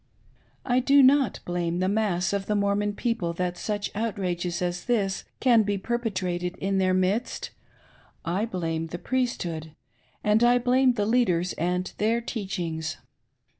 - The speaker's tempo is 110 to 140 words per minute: No, average, 150 wpm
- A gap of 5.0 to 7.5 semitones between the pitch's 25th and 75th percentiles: No, average, 4.6 semitones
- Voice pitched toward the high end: Yes, high, 195 Hz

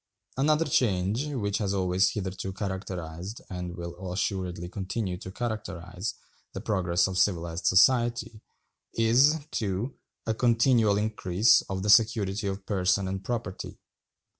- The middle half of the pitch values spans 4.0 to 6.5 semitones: No, average, 3.6 semitones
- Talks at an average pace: No, slow, 125 wpm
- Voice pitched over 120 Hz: No, low, 100 Hz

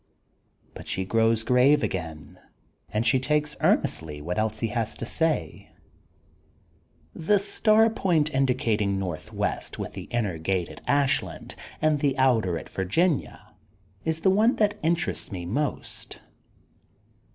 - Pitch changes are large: Yes, wide, 8.2 semitones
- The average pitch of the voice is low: Yes, low, 125 Hz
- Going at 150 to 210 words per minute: No, slow, 135 wpm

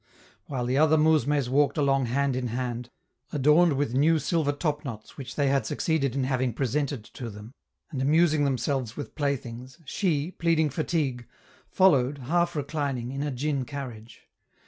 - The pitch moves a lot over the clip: No, average, 3.1 semitones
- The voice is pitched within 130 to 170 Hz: Yes, medium, 140 Hz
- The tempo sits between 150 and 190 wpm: Yes, average, 155 wpm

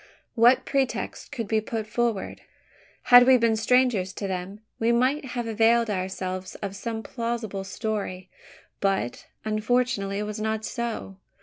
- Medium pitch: No, high, 220 Hz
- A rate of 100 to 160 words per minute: Yes, average, 140 wpm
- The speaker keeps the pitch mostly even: No, average, 3.2 semitones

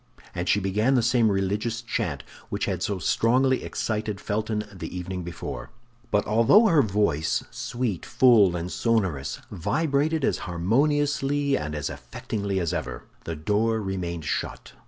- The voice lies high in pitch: No, low, 105 Hz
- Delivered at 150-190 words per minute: No, slow, 135 wpm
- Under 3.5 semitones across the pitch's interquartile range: No, average, 5.3 semitones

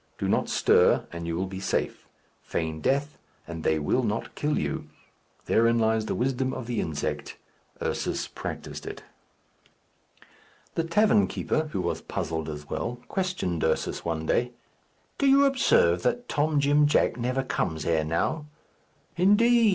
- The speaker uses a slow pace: No, average, 150 wpm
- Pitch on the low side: Yes, low, 120 Hz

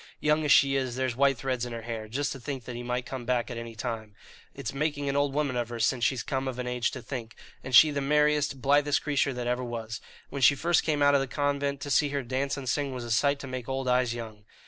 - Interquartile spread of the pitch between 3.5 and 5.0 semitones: No, average, 2.8 semitones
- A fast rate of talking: Yes, fast, 275 wpm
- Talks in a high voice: No, low, 130 Hz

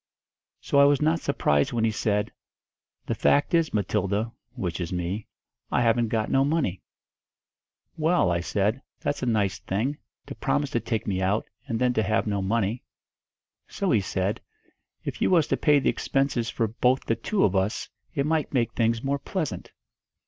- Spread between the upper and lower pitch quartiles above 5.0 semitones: Yes, wide, 5.6 semitones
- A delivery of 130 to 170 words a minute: No, average, 180 wpm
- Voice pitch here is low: Yes, low, 115 Hz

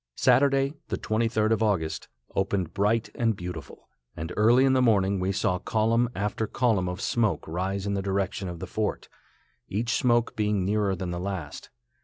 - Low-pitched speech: Yes, low, 100 Hz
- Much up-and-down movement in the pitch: No, average, 3.3 semitones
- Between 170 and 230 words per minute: Yes, average, 175 wpm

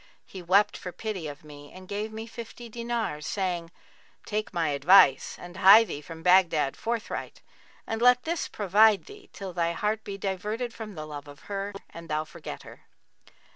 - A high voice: Yes, high, 195 Hz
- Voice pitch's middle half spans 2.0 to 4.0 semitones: No, average, 4.8 semitones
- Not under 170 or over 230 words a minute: Yes, average, 175 wpm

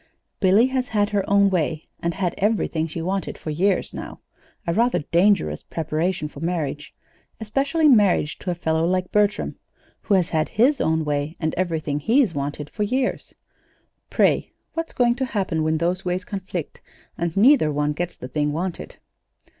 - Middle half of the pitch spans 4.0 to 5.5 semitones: Yes, average, 4.8 semitones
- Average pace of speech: Yes, average, 170 wpm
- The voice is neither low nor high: Yes, medium, 180 Hz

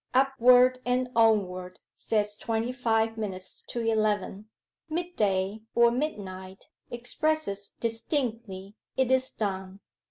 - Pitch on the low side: No, high, 225 Hz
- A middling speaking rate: No, slow, 105 wpm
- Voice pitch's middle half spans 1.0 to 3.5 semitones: No, average, 4.0 semitones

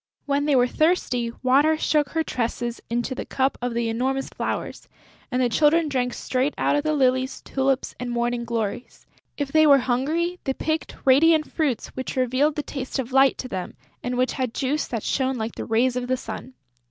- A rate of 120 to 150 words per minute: No, average, 200 wpm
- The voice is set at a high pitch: Yes, very high, 260 Hz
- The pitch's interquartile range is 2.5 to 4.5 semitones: Yes, average, 2.9 semitones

